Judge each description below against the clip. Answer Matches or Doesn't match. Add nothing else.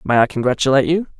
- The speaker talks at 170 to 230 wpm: Matches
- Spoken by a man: Matches